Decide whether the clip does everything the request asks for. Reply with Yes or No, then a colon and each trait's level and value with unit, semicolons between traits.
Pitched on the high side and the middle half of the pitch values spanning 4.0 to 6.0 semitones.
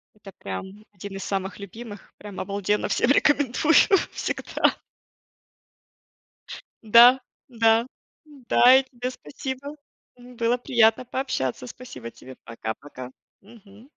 Yes: high, 225 Hz; average, 4.4 semitones